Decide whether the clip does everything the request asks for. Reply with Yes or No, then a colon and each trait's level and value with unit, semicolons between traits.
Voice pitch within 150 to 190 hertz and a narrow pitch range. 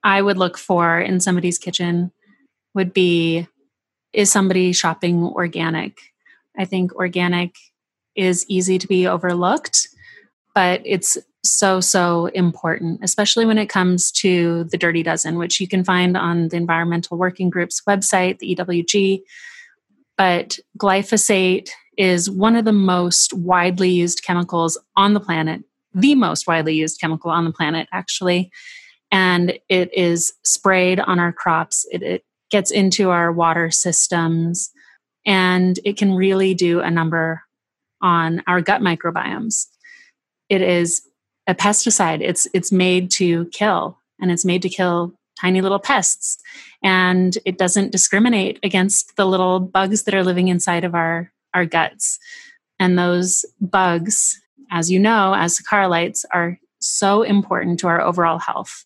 Yes: medium, 185 Hz; narrow, 2.3 semitones